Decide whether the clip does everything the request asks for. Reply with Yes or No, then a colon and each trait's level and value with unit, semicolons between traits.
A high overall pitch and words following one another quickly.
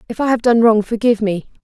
Yes: high, 225 Hz; fast, 255 wpm